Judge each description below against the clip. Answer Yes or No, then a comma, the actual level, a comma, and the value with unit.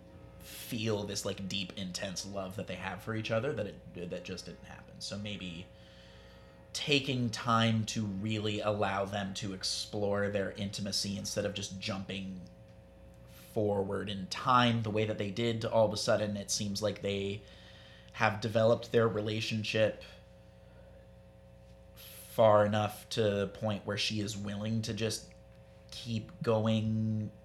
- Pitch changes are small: Yes, narrow, 2.3 semitones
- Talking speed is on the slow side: No, average, 145 wpm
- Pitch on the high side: No, low, 105 Hz